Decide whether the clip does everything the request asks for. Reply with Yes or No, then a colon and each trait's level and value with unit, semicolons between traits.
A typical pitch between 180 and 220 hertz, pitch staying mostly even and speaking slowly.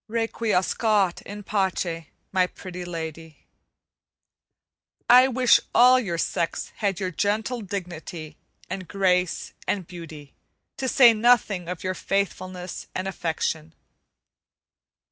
No: medium, 185 Hz; average, 3.7 semitones; slow, 105 wpm